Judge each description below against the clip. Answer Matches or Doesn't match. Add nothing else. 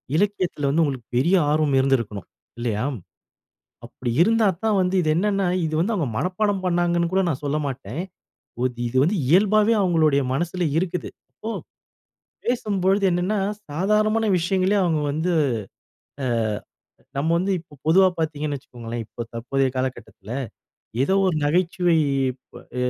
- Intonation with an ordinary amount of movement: Doesn't match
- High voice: Doesn't match